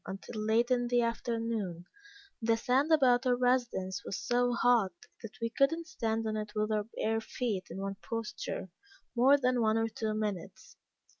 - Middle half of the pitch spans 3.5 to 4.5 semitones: No, narrow, 2.5 semitones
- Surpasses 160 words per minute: Yes, average, 175 wpm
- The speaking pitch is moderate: No, high, 230 Hz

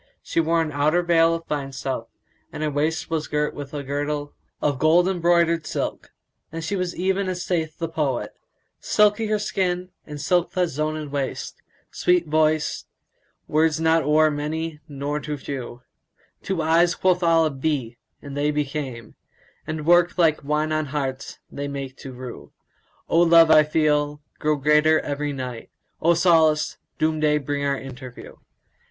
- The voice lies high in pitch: No, medium, 155 Hz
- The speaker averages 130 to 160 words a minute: No, average, 170 wpm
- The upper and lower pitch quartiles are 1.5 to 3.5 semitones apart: Yes, narrow, 2.4 semitones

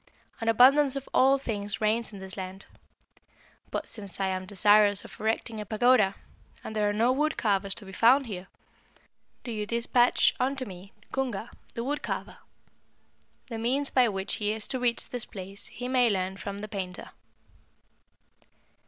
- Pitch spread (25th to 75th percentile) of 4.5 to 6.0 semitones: No, average, 3.8 semitones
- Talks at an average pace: Yes, average, 170 wpm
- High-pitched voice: Yes, high, 215 Hz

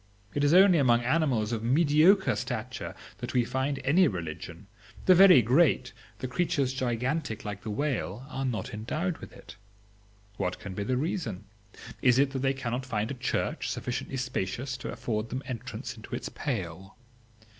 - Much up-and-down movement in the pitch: No, average, 4.3 semitones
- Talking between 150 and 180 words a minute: Yes, average, 165 wpm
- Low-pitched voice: Yes, low, 125 Hz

